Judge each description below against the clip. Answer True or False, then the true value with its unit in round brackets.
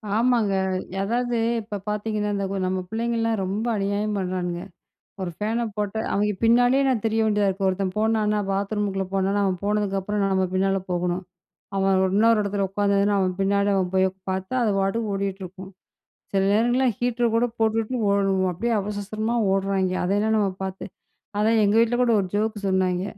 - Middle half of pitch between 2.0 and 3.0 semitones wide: True (2.4 semitones)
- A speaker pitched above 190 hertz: True (205 Hz)